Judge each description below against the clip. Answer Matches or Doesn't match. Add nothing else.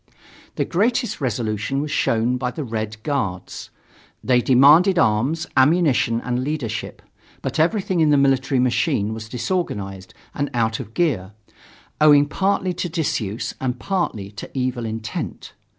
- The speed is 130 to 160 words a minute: Matches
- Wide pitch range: Matches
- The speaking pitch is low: Matches